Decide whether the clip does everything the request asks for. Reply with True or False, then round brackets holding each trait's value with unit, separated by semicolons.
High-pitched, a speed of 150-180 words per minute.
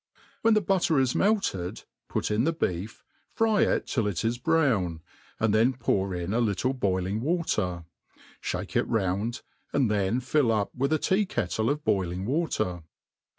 False (115 Hz; 165 wpm)